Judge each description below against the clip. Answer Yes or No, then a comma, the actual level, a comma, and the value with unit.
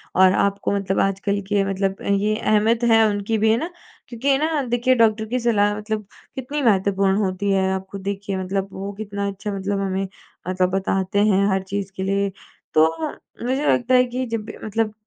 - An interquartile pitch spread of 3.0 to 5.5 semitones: No, narrow, 2.6 semitones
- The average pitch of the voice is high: Yes, high, 200 Hz